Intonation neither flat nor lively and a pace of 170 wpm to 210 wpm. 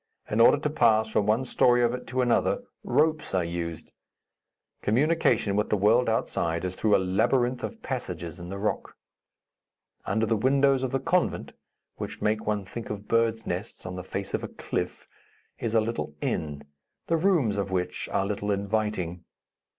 Yes: average, 4.2 semitones; average, 175 wpm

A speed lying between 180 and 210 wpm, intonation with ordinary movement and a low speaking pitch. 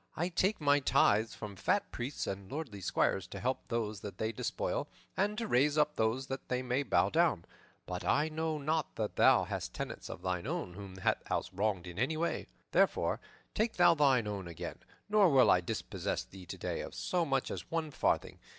No: average, 195 wpm; wide, 7.8 semitones; low, 130 Hz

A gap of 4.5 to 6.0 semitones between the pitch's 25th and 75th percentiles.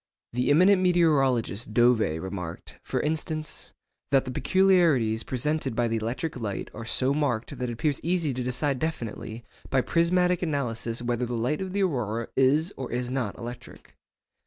Yes: average, 5.2 semitones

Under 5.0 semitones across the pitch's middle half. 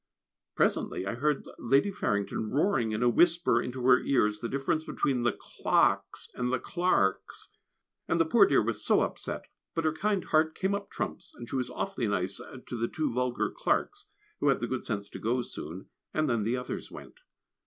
No: wide, 5.6 semitones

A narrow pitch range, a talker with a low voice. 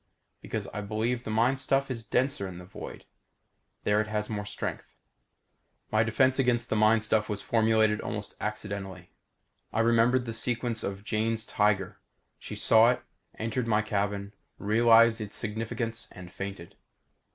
Yes: narrow, 2.0 semitones; low, 110 Hz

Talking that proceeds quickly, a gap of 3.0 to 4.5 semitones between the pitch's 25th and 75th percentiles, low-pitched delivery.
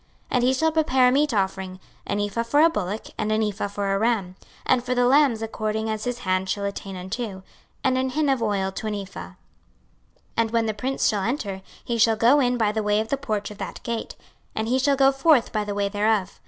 No: fast, 245 wpm; average, 3.8 semitones; high, 220 Hz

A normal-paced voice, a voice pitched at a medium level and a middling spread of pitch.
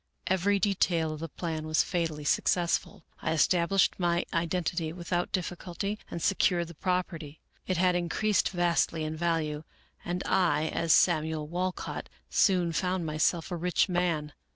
No: average, 155 wpm; medium, 170 Hz; narrow, 2.1 semitones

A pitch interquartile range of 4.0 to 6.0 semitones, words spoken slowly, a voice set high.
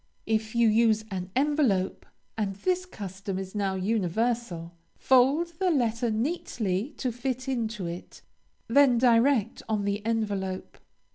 Yes: average, 4.3 semitones; slow, 130 wpm; high, 225 Hz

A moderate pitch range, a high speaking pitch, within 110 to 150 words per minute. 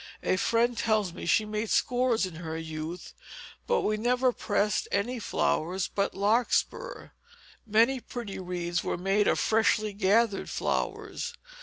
Yes: average, 3.9 semitones; high, 210 Hz; average, 140 wpm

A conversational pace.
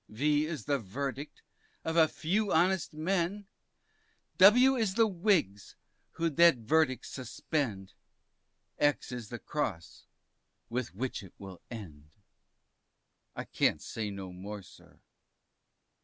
No: slow, 120 wpm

